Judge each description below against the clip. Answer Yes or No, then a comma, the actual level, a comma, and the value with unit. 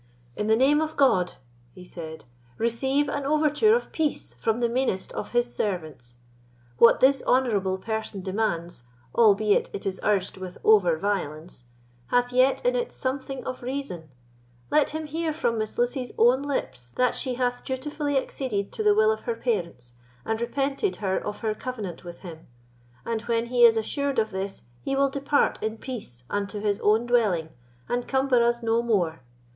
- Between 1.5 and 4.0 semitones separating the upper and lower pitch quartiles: No, wide, 5.6 semitones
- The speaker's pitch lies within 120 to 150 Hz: No, high, 235 Hz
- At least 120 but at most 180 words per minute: Yes, average, 175 wpm